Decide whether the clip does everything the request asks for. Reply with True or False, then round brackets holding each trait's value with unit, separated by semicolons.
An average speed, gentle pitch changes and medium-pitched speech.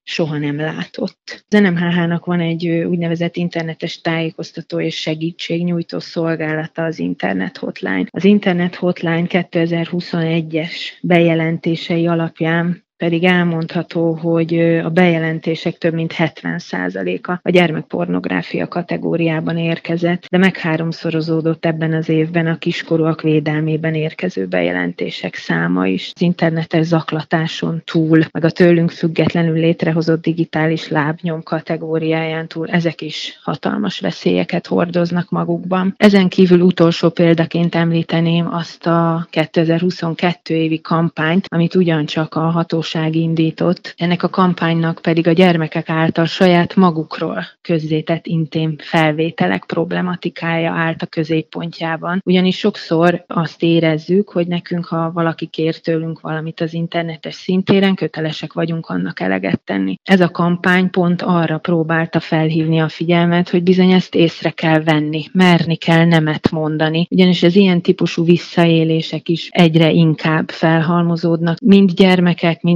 True (120 wpm; 1.3 semitones; 165 Hz)